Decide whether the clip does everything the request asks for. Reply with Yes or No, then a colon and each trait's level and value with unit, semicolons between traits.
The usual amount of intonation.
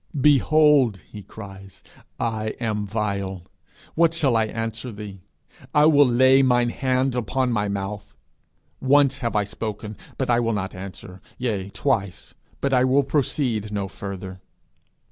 Yes: average, 4.7 semitones